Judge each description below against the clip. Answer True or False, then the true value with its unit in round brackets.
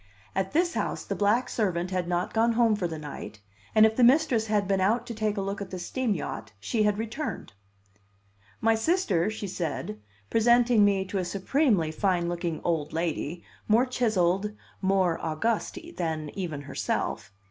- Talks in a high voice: True (195 Hz)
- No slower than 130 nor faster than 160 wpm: False (175 wpm)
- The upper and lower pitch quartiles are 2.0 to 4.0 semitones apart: False (4.6 semitones)